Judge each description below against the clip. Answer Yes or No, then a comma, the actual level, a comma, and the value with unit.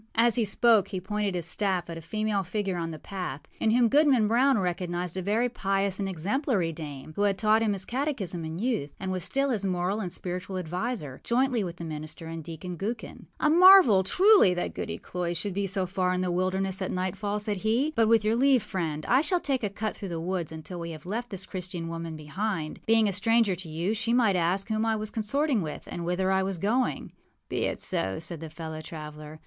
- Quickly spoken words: Yes, fast, 230 wpm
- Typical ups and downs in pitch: Yes, average, 4.3 semitones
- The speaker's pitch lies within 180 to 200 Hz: Yes, high, 190 Hz